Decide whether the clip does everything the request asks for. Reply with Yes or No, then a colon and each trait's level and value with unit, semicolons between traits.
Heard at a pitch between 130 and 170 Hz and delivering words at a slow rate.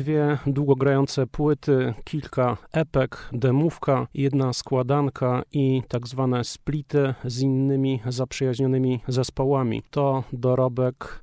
Yes: low, 135 Hz; slow, 95 wpm